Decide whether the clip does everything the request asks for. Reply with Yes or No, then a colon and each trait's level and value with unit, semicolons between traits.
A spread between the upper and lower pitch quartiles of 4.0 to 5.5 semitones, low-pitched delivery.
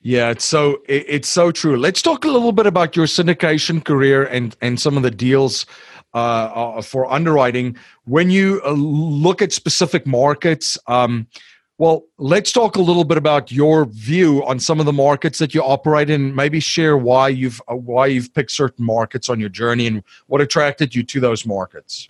No: average, 4.6 semitones; medium, 145 Hz